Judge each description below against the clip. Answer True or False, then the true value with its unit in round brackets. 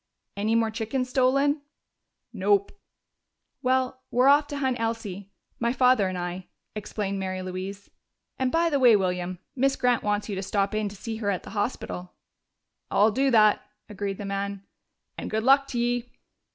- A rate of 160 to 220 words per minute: True (170 wpm)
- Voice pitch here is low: False (215 Hz)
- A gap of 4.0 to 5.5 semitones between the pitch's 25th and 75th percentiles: True (4.3 semitones)